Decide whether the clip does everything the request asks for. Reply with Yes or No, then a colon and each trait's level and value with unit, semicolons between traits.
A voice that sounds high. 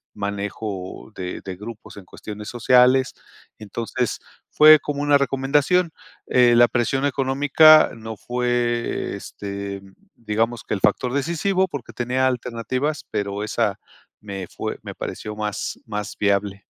No: low, 120 Hz